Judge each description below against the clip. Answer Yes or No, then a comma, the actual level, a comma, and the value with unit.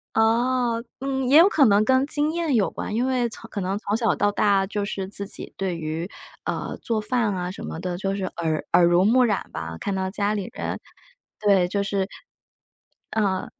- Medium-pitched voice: No, high, 205 Hz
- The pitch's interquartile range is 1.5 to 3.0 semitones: No, average, 4.2 semitones